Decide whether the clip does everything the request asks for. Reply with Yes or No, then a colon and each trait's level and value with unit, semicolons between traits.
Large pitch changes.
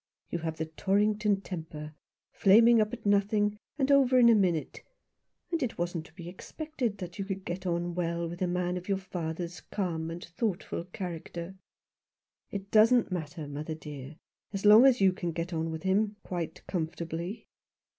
No: average, 3.7 semitones